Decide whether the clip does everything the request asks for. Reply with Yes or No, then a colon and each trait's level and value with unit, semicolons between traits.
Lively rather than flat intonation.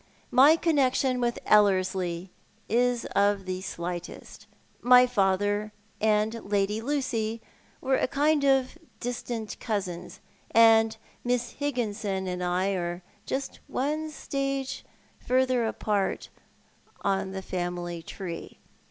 No: average, 4.9 semitones